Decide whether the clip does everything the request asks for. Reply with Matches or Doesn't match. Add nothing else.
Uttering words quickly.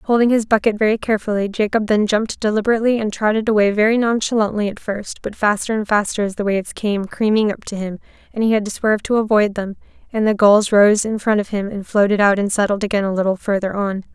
Matches